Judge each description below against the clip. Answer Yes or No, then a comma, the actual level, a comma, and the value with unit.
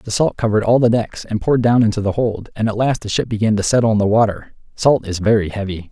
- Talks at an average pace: No, fast, 275 wpm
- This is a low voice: Yes, low, 110 Hz